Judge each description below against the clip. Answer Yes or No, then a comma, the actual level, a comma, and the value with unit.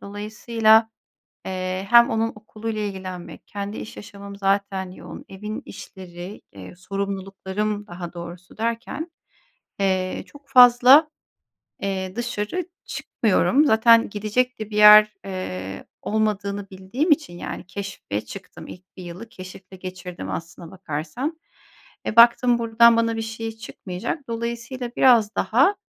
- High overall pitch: Yes, high, 205 Hz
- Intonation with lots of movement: No, average, 3.7 semitones